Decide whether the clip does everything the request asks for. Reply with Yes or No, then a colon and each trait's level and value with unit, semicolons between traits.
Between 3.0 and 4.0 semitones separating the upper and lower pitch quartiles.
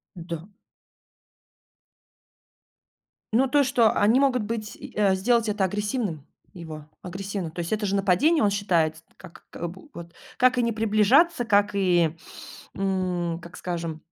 No: average, 4.5 semitones